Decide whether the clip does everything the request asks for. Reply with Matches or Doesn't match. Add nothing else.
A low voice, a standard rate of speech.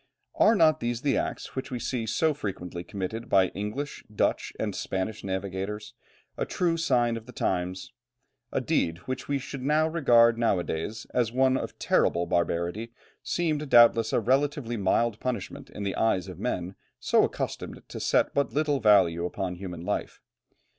Matches